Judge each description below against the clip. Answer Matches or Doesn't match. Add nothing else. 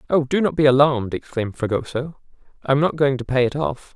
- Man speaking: Matches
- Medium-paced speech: Doesn't match